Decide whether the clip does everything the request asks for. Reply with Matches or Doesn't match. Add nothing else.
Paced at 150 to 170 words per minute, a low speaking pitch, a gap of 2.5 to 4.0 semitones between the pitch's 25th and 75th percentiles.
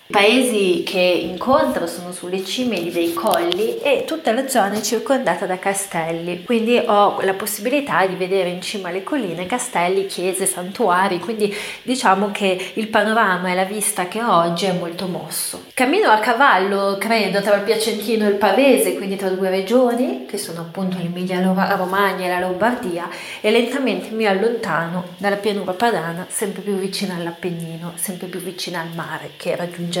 Doesn't match